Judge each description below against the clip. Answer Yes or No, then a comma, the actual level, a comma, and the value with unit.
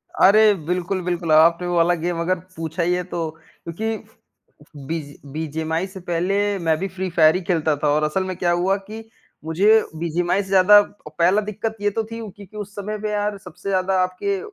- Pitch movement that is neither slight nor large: Yes, average, 3.3 semitones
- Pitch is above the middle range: No, medium, 180 Hz